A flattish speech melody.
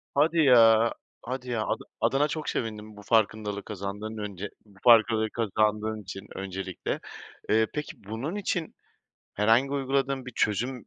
No: average, 3.9 semitones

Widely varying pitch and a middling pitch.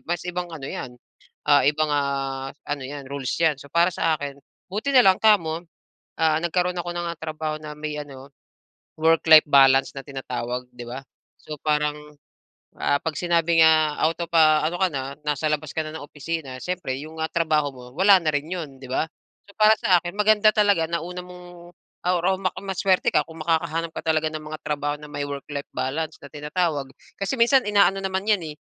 No: average, 3.4 semitones; medium, 160 Hz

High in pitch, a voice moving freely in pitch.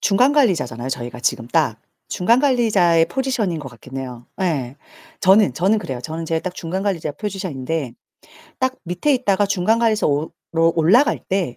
No: medium, 175 Hz; wide, 7.3 semitones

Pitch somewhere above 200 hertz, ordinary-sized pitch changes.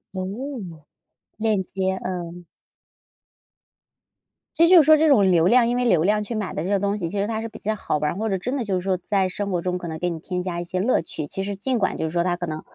No: high, 190 Hz; average, 3.5 semitones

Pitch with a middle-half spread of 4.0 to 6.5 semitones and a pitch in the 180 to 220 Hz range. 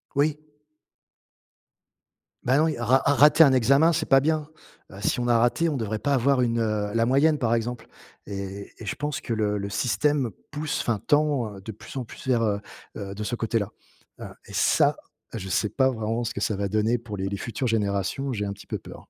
No: average, 4.8 semitones; low, 115 Hz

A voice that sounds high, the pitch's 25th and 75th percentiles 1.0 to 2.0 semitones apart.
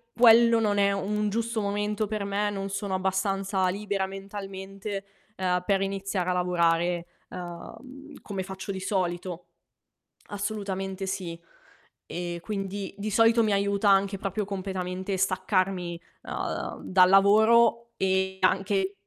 Yes: high, 195 Hz; narrow, 1.7 semitones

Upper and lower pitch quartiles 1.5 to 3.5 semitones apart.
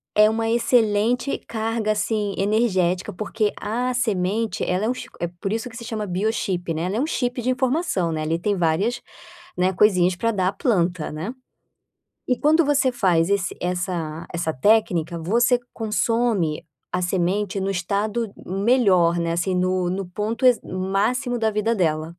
No: average, 4.2 semitones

